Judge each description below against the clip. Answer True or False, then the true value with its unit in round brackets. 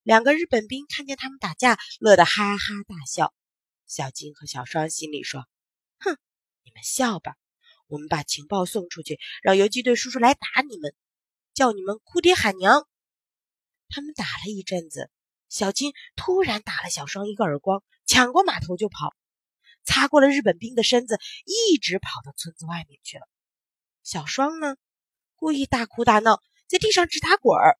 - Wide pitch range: True (8.9 semitones)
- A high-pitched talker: True (215 Hz)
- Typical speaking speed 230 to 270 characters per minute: True (250 characters per minute)